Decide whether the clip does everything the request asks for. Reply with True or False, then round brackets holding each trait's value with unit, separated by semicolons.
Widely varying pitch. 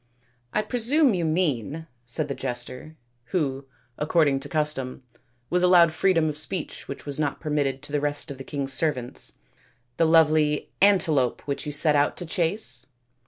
False (3.4 semitones)